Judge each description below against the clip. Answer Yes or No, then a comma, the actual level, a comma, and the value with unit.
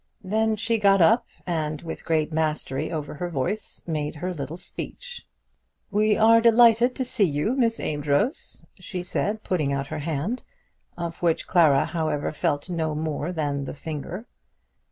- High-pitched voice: No, medium, 170 Hz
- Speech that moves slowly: No, average, 155 wpm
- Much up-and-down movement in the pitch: Yes, wide, 6.2 semitones